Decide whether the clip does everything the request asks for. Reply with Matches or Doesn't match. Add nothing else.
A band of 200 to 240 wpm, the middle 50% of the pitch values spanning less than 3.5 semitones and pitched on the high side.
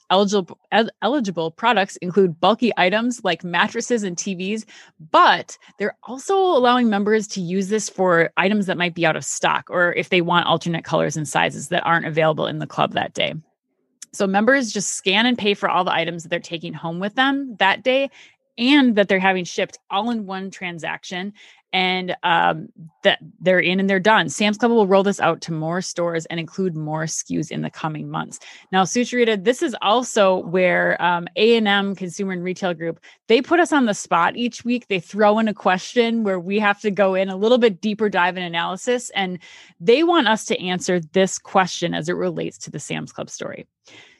Doesn't match